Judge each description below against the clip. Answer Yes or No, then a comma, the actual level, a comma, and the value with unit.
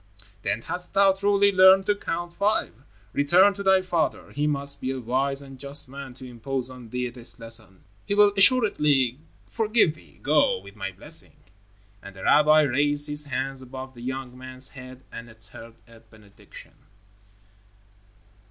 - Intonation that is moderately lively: No, wide, 5.7 semitones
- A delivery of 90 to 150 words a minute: No, average, 160 wpm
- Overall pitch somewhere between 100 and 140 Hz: Yes, low, 135 Hz